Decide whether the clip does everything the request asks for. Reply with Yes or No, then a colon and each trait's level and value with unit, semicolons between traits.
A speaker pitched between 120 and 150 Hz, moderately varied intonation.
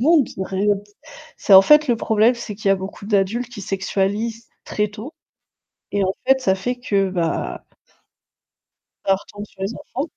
No: high, 210 Hz; average, 3.6 semitones